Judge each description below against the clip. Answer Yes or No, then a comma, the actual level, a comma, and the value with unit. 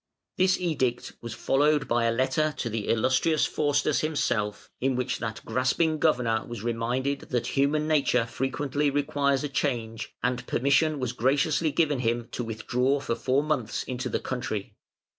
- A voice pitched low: Yes, low, 130 Hz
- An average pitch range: Yes, average, 3.6 semitones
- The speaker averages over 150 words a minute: Yes, average, 160 wpm